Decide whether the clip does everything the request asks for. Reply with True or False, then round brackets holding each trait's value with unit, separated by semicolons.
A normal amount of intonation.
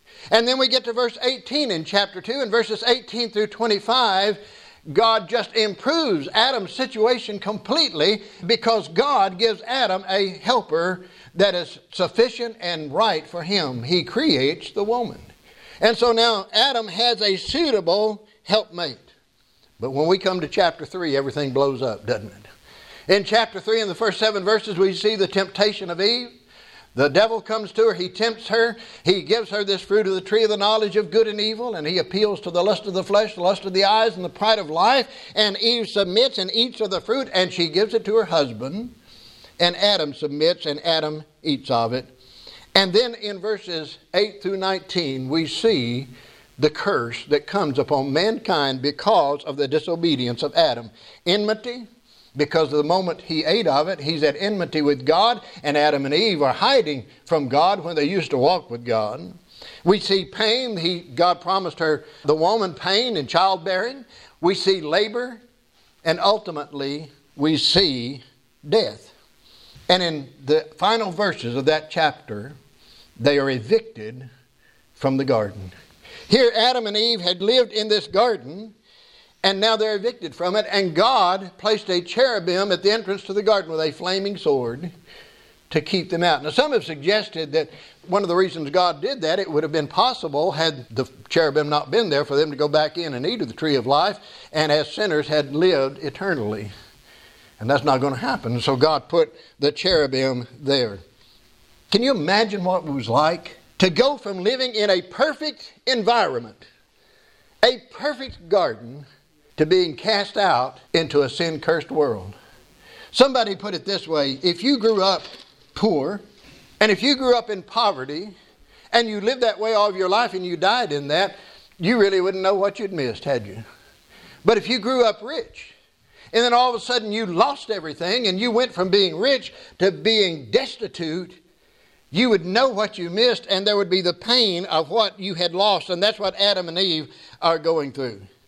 False (6.0 semitones)